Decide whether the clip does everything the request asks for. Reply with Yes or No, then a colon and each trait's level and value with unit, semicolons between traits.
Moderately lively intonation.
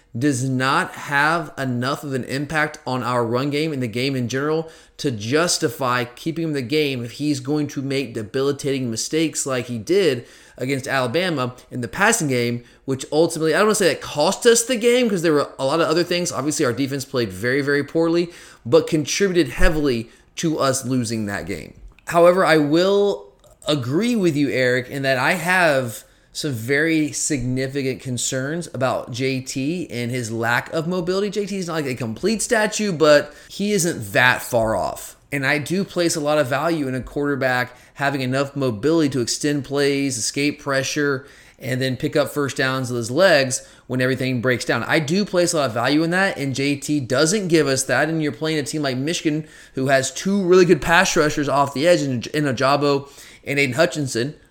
Yes: average, 3.7 semitones